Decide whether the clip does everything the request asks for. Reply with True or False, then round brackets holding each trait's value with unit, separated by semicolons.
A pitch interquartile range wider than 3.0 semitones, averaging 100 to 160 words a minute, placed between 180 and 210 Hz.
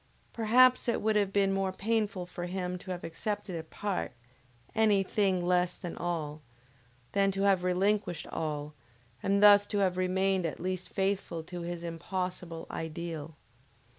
False (2.6 semitones; 155 wpm; 185 Hz)